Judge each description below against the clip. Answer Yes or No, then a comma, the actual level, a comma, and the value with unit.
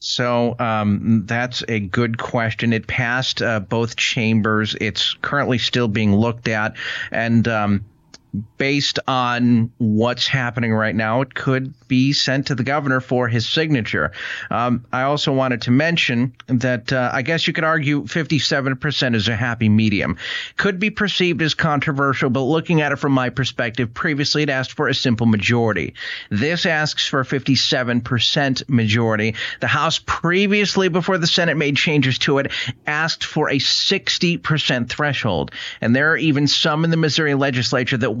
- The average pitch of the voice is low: Yes, low, 130 Hz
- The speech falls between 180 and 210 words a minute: No, average, 160 wpm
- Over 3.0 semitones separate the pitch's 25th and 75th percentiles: Yes, average, 4.1 semitones